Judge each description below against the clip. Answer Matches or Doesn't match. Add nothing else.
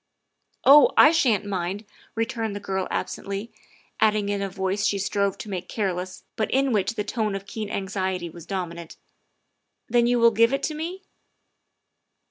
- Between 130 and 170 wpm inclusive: Doesn't match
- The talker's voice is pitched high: Matches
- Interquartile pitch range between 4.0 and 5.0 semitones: Doesn't match